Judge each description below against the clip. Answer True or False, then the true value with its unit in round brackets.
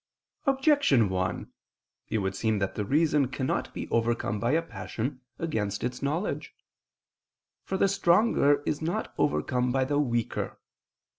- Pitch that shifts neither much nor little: False (6.5 semitones)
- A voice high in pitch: False (130 Hz)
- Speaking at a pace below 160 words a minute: True (140 wpm)